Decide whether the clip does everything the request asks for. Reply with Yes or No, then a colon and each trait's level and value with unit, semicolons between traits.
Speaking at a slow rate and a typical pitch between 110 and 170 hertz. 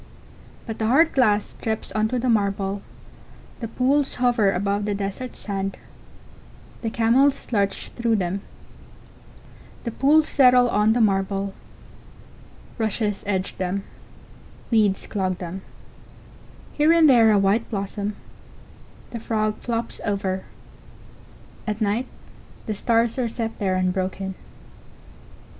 No: slow, 120 wpm; high, 215 Hz